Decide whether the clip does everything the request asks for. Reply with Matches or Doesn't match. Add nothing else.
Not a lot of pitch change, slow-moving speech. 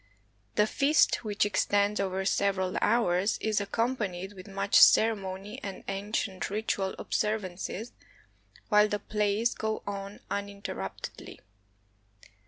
Matches